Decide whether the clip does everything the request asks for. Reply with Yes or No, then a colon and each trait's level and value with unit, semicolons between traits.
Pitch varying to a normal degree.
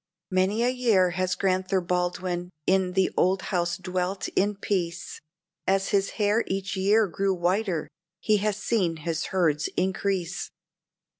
No: narrow, 1.8 semitones